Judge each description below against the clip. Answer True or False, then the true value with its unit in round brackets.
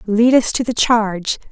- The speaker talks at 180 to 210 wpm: True (200 wpm)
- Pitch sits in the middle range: False (220 Hz)